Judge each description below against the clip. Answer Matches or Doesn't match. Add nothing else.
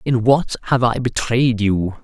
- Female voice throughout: Doesn't match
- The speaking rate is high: Doesn't match